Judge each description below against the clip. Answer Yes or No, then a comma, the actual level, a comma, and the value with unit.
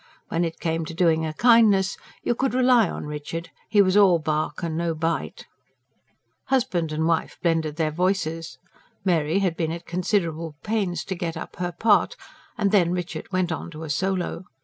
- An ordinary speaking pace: Yes, average, 180 wpm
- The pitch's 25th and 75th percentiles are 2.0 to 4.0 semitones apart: Yes, average, 3.0 semitones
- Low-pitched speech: No, medium, 170 Hz